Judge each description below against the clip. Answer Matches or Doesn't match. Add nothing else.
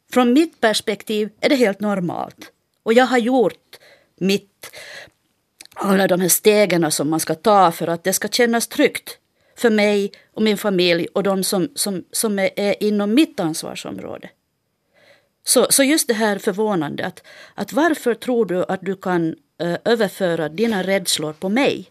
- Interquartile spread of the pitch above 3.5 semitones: Matches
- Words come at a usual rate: Doesn't match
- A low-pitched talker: Doesn't match